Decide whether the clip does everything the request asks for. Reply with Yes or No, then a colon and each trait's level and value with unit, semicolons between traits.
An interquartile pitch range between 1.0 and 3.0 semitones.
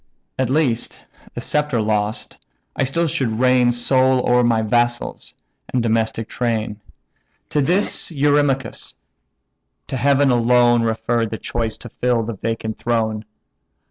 Yes: average, 2.7 semitones